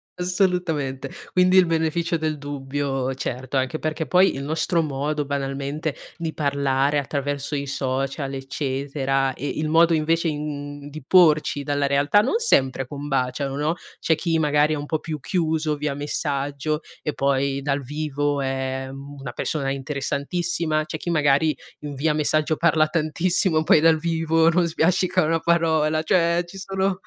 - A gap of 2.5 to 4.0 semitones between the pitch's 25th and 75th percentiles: Yes, average, 2.8 semitones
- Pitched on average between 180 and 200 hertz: No, medium, 150 Hz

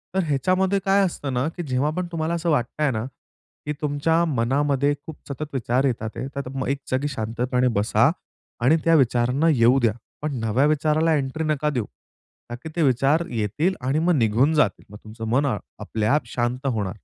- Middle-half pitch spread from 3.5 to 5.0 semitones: Yes, average, 4.1 semitones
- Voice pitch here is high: No, medium, 140 Hz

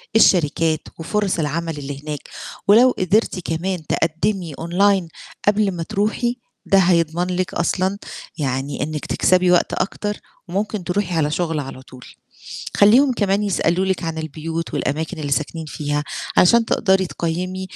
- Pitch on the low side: No, medium, 175 Hz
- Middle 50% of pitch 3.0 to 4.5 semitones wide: Yes, average, 3.7 semitones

